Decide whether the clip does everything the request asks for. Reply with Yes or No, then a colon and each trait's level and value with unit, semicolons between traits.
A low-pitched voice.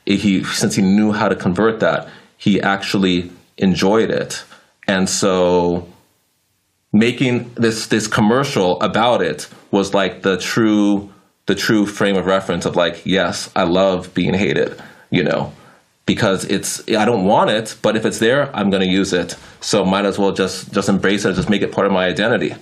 Yes: low, 100 Hz